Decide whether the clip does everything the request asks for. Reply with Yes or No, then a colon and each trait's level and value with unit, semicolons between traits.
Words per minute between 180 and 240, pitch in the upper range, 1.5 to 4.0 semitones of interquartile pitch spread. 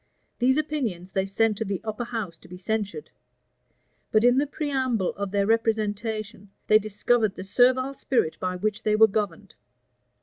No: average, 165 wpm; high, 215 Hz; average, 3.4 semitones